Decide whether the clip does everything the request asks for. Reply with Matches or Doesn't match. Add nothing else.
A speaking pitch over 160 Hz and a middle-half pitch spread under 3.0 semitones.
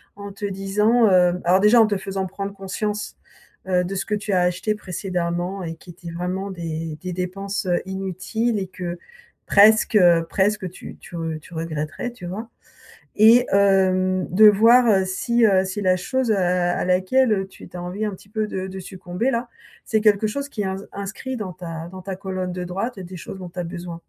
Matches